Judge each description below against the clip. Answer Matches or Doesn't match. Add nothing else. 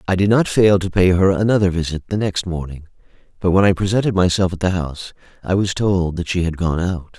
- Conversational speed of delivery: Doesn't match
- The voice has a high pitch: Doesn't match